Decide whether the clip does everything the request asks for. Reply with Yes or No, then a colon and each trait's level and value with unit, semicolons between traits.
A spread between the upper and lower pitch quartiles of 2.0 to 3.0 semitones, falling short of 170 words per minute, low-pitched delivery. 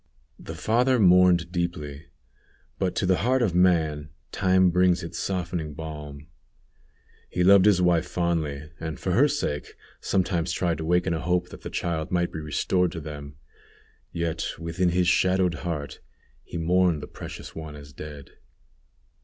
Yes: narrow, 2.6 semitones; average, 155 wpm; very low, 85 Hz